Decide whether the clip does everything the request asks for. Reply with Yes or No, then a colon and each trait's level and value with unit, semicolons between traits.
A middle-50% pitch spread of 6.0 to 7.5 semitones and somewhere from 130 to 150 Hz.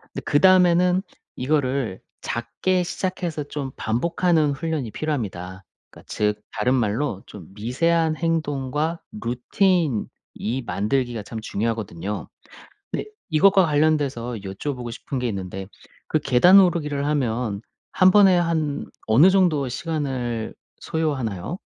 Yes: wide, 6.3 semitones; medium, 140 Hz